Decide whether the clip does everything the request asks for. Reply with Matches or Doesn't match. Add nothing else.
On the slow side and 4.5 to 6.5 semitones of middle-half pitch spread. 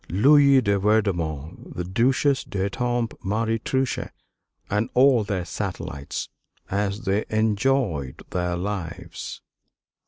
Matches